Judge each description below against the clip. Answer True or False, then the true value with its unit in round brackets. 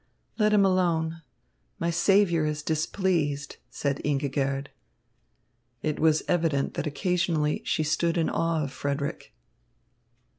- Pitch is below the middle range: False (160 Hz)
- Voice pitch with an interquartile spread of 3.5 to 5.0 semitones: False (3.0 semitones)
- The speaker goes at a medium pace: False (115 wpm)